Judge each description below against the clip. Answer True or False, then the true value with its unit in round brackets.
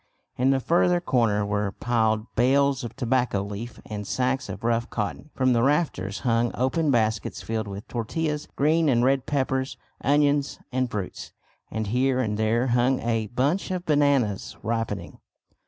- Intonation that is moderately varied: True (3.9 semitones)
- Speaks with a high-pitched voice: False (125 Hz)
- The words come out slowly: False (155 wpm)